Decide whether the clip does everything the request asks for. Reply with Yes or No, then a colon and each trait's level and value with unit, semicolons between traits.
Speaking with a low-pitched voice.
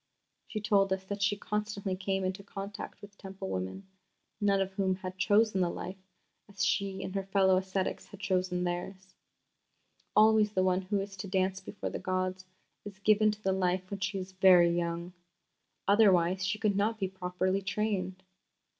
No: high, 190 Hz